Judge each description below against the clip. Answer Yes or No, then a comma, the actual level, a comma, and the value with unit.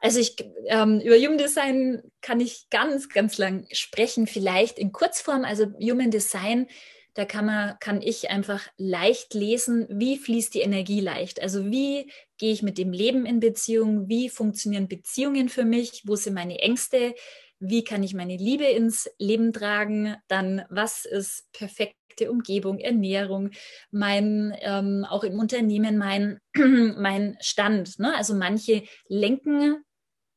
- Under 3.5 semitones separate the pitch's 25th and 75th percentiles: Yes, average, 3.0 semitones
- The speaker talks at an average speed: Yes, average, 150 wpm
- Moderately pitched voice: No, high, 215 Hz